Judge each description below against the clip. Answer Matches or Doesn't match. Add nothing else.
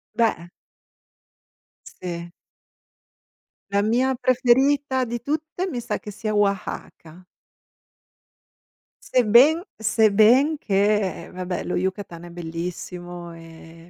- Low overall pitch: Doesn't match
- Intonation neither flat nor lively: Doesn't match